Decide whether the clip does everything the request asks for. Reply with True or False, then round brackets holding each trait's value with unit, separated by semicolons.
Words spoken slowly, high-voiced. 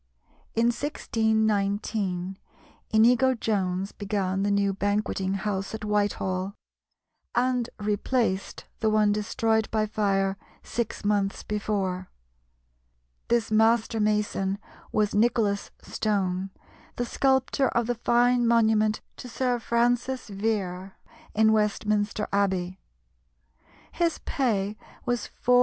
True (105 wpm; 215 Hz)